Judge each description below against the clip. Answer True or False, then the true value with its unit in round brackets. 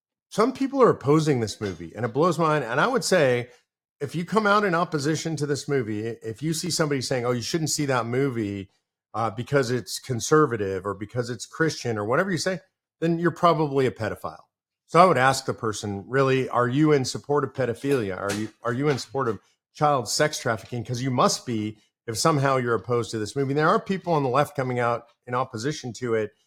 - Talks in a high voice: False (135 Hz)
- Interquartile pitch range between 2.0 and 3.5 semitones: False (4.8 semitones)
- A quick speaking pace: True (225 wpm)